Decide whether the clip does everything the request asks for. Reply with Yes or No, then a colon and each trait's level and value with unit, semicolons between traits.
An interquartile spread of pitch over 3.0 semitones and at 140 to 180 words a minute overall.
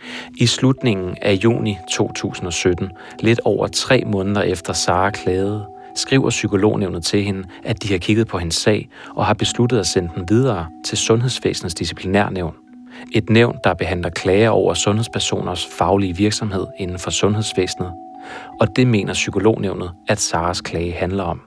Yes: average, 3.5 semitones; average, 150 wpm